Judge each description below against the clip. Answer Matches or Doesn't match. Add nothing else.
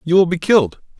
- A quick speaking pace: Matches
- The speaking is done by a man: Matches